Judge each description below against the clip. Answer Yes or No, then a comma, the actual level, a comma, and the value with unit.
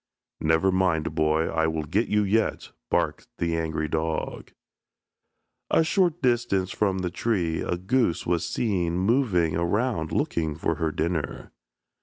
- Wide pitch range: No, average, 4.6 semitones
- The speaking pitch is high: No, very low, 85 Hz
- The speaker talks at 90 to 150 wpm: Yes, average, 140 wpm